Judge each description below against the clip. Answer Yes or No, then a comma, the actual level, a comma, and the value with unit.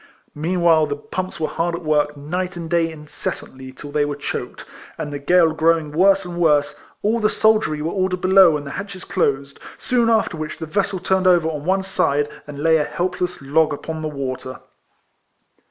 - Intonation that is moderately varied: Yes, average, 3.9 semitones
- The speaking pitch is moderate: Yes, medium, 160 Hz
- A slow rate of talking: No, average, 195 wpm